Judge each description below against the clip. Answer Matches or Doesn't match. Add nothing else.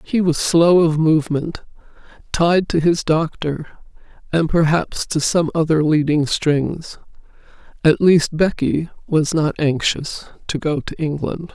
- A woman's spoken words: Matches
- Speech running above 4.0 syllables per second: Doesn't match